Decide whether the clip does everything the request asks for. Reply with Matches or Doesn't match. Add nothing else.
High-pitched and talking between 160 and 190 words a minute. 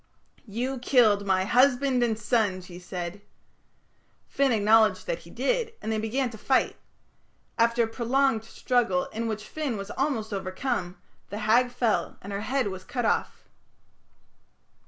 Doesn't match